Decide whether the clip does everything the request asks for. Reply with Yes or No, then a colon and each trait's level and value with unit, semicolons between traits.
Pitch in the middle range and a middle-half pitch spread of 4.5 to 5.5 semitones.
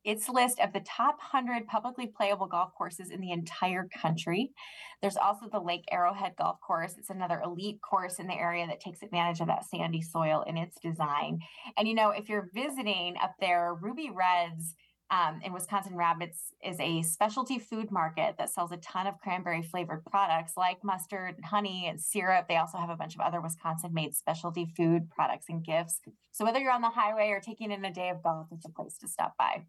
No: medium, 180 Hz; average, 3.6 semitones